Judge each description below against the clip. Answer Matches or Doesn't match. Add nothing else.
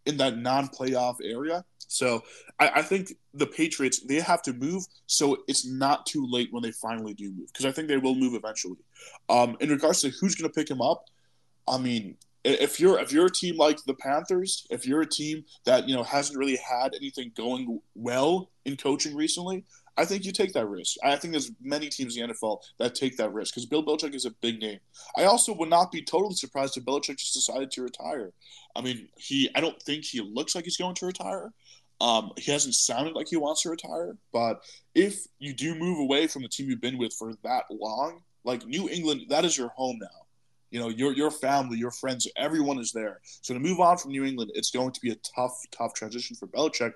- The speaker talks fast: Matches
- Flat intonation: Doesn't match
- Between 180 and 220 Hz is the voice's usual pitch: Doesn't match